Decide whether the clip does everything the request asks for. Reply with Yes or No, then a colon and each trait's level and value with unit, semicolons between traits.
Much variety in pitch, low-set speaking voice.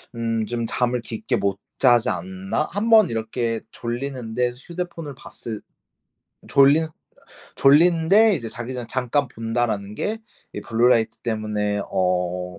No: average, 4.2 semitones; low, 120 Hz